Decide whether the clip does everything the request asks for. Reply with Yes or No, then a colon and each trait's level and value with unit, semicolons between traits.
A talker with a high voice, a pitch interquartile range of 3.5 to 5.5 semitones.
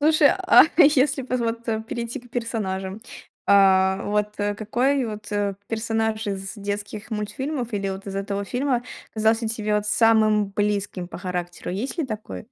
No: high, 215 Hz; average, 2.8 semitones